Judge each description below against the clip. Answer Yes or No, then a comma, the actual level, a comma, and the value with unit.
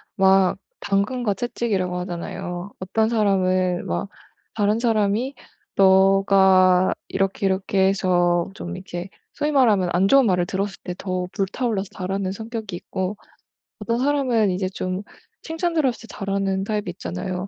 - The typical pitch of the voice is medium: No, high, 195 Hz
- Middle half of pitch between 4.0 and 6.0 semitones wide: No, average, 2.8 semitones